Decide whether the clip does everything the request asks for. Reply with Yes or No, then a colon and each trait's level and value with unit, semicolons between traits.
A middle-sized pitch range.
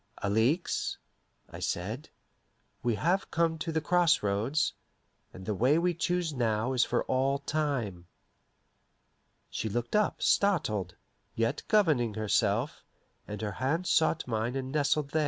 No: wide, 6.6 semitones